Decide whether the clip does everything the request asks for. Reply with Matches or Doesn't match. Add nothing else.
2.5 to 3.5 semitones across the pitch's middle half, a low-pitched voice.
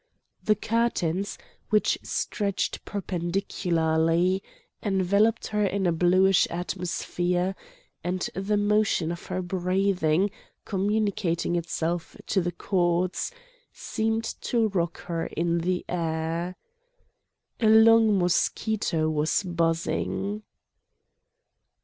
Doesn't match